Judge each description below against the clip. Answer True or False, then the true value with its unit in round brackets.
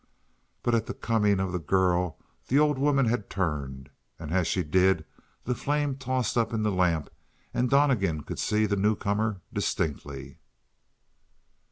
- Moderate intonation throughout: False (5.7 semitones)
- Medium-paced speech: True (155 wpm)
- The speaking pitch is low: True (100 Hz)